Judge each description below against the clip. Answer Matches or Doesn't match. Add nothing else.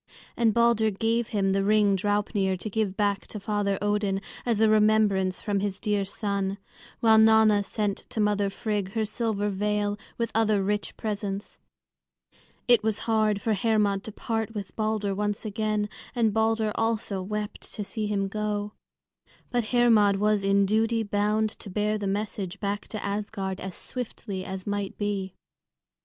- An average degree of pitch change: Doesn't match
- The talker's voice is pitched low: Doesn't match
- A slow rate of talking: Doesn't match